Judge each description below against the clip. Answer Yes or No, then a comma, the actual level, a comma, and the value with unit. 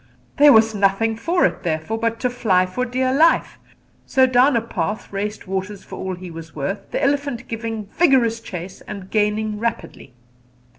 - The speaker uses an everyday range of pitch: Yes, average, 4.3 semitones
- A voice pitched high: Yes, high, 220 Hz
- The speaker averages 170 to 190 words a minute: Yes, average, 175 wpm